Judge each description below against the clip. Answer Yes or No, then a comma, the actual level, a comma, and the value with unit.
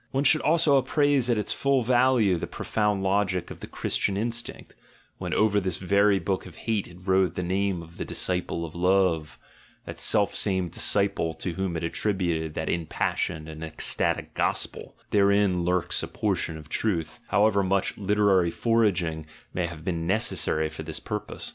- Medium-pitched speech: No, very low, 95 Hz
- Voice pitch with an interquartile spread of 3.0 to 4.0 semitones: Yes, average, 3.7 semitones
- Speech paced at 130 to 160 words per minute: No, average, 175 wpm